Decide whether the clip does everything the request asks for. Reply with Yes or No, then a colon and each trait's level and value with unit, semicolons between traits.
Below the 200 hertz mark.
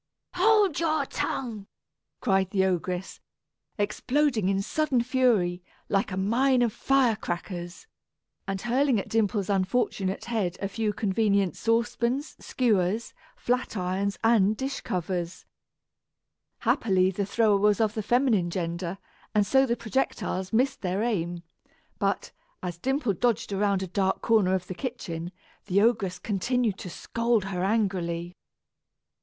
No: high, 205 Hz